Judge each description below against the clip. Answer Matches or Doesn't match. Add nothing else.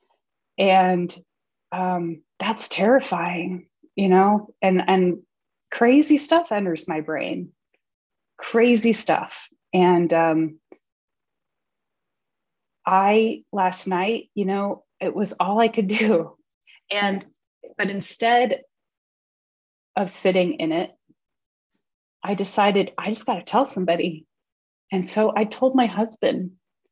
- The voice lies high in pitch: Matches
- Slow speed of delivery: Matches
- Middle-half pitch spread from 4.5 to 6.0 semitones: Doesn't match